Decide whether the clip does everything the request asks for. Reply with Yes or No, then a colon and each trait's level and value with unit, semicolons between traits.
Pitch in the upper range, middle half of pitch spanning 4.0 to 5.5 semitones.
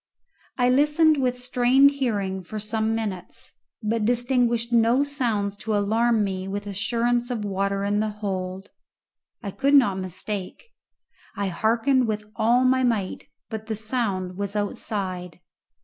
No: high, 220 Hz; average, 3.5 semitones